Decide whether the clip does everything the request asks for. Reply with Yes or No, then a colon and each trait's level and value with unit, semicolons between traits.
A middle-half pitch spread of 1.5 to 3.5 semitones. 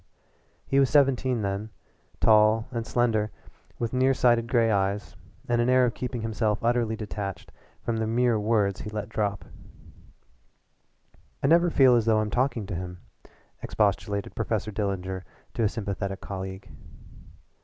Yes: average, 3.0 semitones